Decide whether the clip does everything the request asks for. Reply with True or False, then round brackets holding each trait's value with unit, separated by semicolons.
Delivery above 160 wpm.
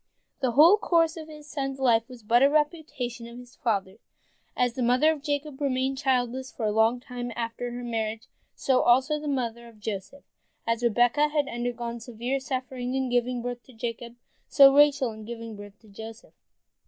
True (185 wpm)